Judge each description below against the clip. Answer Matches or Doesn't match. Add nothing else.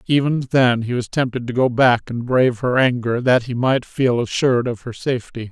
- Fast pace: Matches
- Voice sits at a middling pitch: Doesn't match